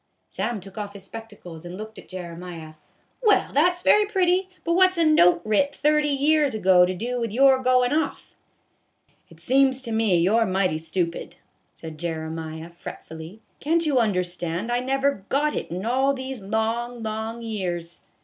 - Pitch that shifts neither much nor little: No, wide, 7.2 semitones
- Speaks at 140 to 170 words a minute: No, average, 195 wpm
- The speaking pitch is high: Yes, high, 220 Hz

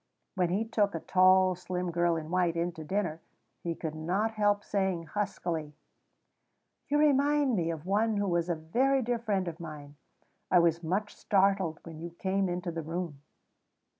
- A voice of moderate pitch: Yes, medium, 180 Hz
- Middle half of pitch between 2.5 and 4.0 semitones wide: Yes, average, 3.5 semitones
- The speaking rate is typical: Yes, average, 175 wpm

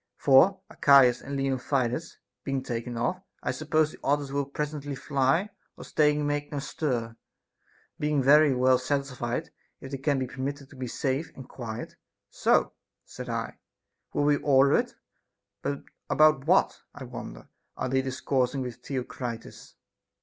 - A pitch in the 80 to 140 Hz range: Yes, low, 135 Hz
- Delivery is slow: No, average, 155 wpm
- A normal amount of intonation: No, narrow, 2.3 semitones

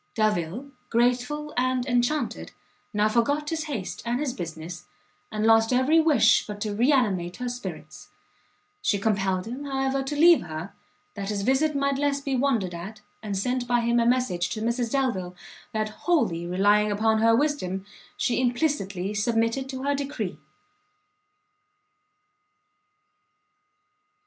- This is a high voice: Yes, high, 235 Hz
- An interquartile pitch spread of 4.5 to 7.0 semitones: Yes, average, 4.8 semitones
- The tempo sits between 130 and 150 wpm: Yes, average, 140 wpm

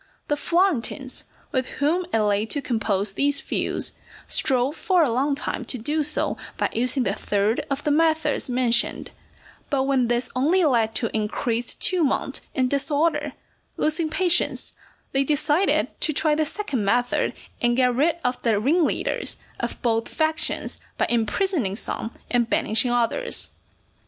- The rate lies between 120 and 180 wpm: Yes, average, 150 wpm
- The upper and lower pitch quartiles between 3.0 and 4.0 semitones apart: No, average, 4.7 semitones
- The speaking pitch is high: Yes, very high, 265 Hz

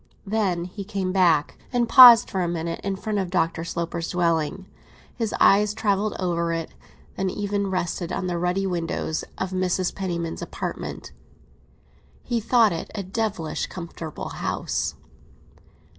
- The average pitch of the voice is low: No, medium, 185 Hz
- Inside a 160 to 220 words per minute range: No, average, 145 wpm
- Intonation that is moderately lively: Yes, average, 3.1 semitones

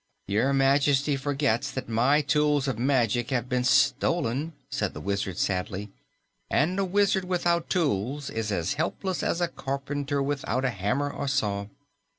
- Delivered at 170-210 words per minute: No, average, 155 wpm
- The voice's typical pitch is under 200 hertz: Yes, low, 135 Hz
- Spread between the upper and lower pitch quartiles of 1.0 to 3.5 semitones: No, average, 4.1 semitones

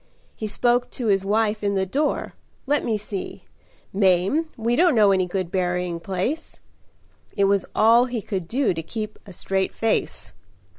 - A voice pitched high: Yes, high, 205 Hz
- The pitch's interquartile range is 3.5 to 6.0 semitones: Yes, average, 3.9 semitones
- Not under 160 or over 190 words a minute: Yes, average, 165 wpm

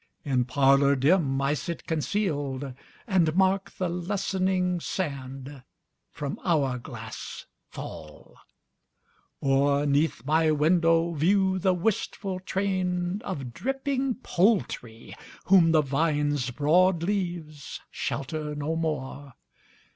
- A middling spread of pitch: Yes, average, 4.8 semitones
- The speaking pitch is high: No, medium, 160 Hz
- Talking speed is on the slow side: Yes, slow, 100 wpm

